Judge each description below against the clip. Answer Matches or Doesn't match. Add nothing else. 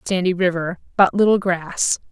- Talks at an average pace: Doesn't match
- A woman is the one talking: Matches